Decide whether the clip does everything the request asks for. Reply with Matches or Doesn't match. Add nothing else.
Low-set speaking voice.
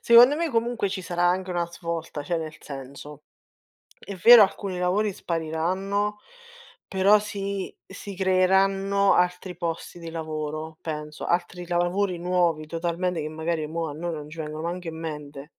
Doesn't match